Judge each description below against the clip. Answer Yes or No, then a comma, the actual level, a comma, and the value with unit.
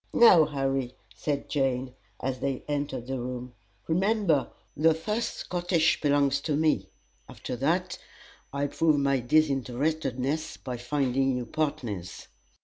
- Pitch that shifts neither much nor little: Yes, average, 3.5 semitones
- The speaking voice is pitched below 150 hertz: Yes, medium, 140 Hz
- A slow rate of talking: Yes, slow, 125 wpm